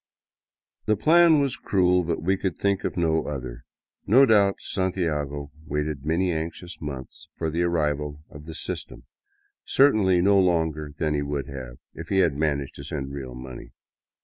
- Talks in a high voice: No, very low, 80 Hz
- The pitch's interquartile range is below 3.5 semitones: No, average, 4.6 semitones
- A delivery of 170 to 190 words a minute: Yes, average, 175 wpm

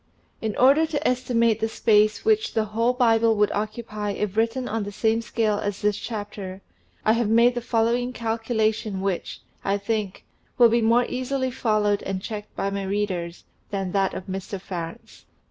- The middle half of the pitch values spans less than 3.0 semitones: Yes, narrow, 2.5 semitones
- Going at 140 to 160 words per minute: No, average, 175 wpm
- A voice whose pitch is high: Yes, high, 220 Hz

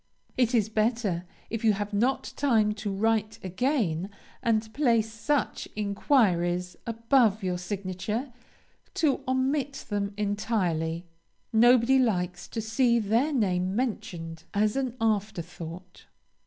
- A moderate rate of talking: No, slow, 115 wpm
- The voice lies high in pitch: Yes, high, 215 Hz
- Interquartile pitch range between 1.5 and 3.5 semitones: No, average, 4.2 semitones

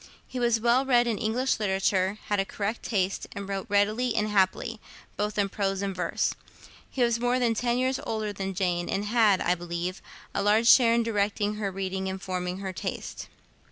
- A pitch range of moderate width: Yes, average, 3.3 semitones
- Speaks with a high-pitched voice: Yes, high, 205 Hz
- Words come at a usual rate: Yes, average, 195 wpm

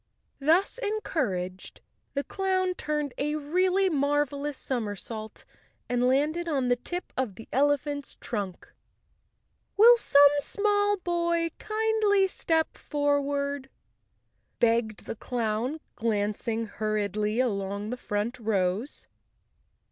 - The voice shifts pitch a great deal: Yes, wide, 7.4 semitones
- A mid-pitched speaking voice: No, very high, 280 Hz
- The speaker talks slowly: Yes, slow, 110 wpm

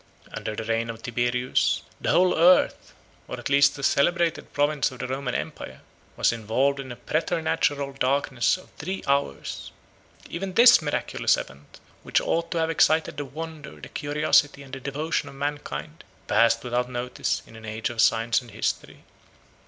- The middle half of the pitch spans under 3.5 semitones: No, average, 4.3 semitones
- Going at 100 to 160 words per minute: No, average, 175 wpm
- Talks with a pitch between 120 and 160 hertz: Yes, medium, 140 Hz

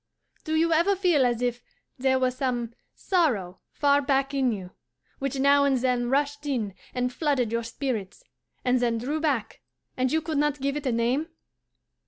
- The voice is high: Yes, very high, 265 Hz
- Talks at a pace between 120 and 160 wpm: No, average, 180 wpm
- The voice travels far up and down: No, average, 3.1 semitones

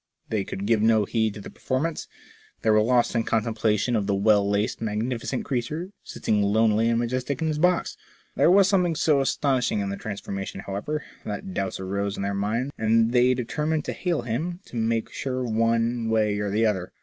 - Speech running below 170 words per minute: No, average, 195 wpm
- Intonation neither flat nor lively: Yes, average, 3.7 semitones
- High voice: No, low, 115 Hz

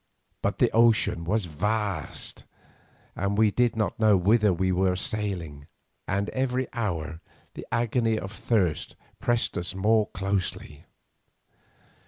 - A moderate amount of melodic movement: Yes, average, 3.6 semitones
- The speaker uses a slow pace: Yes, slow, 125 wpm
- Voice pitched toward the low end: Yes, low, 100 Hz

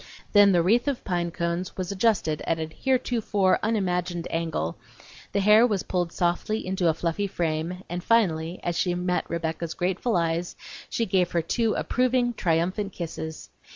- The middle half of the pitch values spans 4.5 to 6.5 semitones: No, average, 3.5 semitones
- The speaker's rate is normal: Yes, average, 160 wpm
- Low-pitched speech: No, medium, 180 Hz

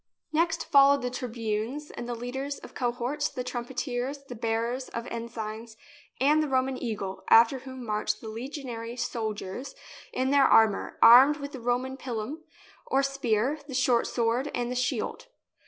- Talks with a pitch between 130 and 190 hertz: No, high, 245 Hz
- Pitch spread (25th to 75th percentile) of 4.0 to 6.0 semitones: No, average, 2.8 semitones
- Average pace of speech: Yes, average, 155 wpm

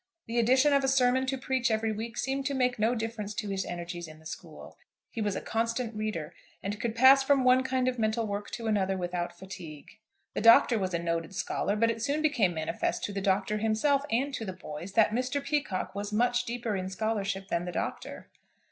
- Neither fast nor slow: No, fast, 220 wpm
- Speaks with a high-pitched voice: Yes, high, 220 Hz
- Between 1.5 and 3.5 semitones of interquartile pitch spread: No, average, 4.5 semitones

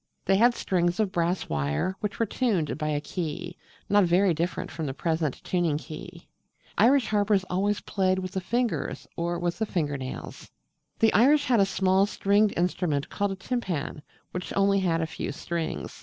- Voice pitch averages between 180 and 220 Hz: Yes, medium, 185 Hz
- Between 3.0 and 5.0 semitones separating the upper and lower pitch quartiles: Yes, average, 3.6 semitones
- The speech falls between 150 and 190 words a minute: Yes, average, 180 wpm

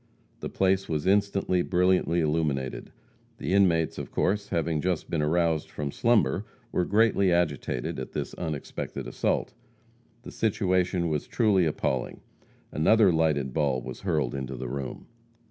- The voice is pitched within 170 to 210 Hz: No, very low, 85 Hz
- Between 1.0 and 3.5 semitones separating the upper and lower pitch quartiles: No, average, 4.2 semitones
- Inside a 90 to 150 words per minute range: Yes, average, 140 wpm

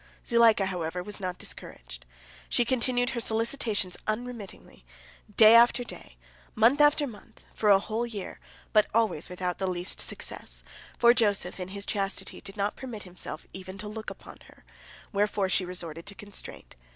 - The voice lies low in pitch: No, high, 205 Hz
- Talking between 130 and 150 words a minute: No, average, 160 wpm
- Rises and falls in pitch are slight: No, average, 3.7 semitones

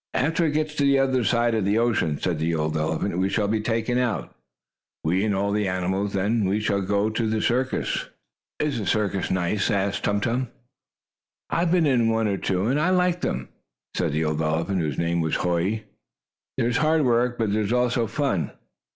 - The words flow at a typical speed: No, fast, 210 wpm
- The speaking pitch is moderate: No, low, 105 Hz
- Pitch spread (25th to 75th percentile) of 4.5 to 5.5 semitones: Yes, average, 4.8 semitones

